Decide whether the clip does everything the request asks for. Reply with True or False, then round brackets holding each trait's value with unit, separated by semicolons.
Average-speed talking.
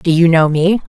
False (255 wpm)